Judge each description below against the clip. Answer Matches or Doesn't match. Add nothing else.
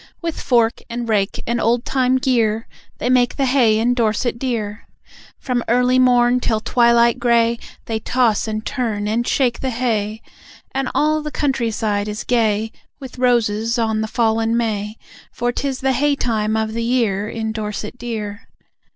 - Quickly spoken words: Doesn't match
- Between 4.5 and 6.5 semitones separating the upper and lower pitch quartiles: Doesn't match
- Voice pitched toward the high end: Matches